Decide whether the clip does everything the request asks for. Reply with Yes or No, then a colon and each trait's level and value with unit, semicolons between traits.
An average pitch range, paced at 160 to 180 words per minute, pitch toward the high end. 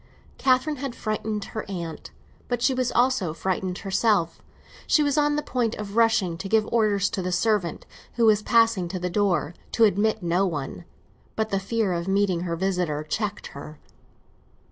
Yes: average, 4.1 semitones; average, 175 wpm; high, 205 Hz